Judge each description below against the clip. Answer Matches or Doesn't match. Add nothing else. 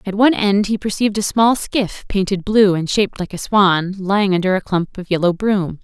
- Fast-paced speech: Matches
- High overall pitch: Matches